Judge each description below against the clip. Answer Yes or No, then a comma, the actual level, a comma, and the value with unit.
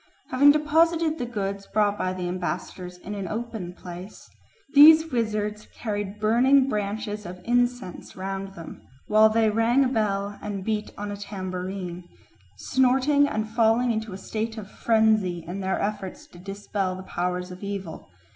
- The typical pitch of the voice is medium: No, high, 210 Hz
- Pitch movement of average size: Yes, average, 3.6 semitones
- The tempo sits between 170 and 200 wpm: No, average, 155 wpm